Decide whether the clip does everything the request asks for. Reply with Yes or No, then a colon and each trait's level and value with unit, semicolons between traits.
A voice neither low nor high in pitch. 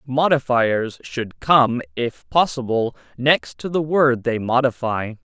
No: low, 125 Hz